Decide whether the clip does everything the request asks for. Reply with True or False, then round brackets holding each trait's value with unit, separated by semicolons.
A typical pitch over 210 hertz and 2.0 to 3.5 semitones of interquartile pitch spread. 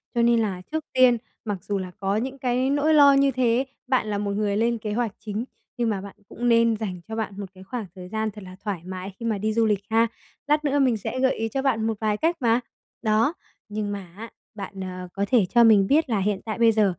True (220 Hz; 3.2 semitones)